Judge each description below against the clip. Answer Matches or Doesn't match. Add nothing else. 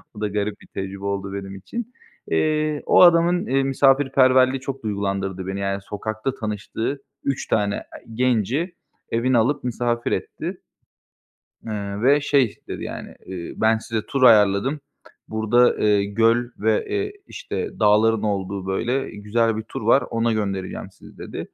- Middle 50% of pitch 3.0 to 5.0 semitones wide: Matches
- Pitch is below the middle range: Matches